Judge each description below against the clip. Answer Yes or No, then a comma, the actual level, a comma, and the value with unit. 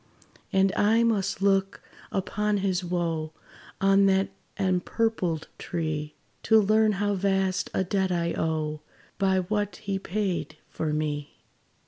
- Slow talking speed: Yes, slow, 125 wpm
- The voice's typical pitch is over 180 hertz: Yes, high, 190 Hz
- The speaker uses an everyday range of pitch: Yes, average, 3.0 semitones